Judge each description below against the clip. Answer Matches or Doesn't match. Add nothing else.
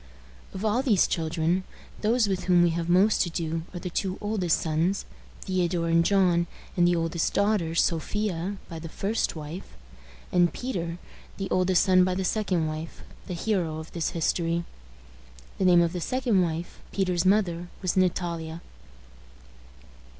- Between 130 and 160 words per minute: Matches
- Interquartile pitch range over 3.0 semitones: Doesn't match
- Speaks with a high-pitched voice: Doesn't match